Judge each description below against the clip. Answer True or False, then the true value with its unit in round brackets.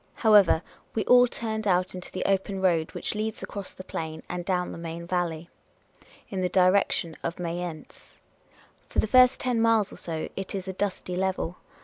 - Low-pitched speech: False (185 Hz)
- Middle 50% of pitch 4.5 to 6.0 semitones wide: False (3.2 semitones)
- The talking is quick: False (185 wpm)